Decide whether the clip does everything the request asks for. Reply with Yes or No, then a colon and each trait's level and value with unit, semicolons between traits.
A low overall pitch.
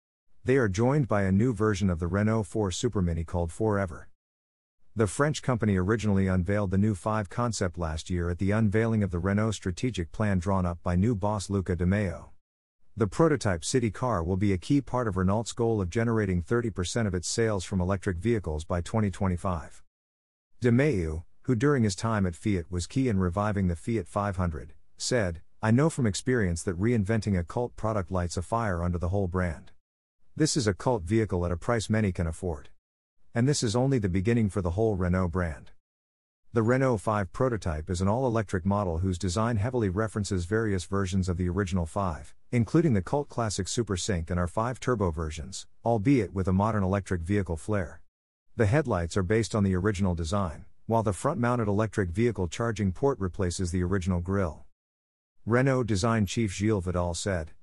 Yes: low, 100 Hz